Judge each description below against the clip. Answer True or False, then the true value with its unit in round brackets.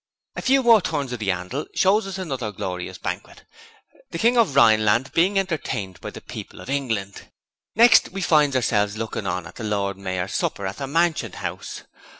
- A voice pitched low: True (130 Hz)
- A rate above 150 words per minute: True (185 wpm)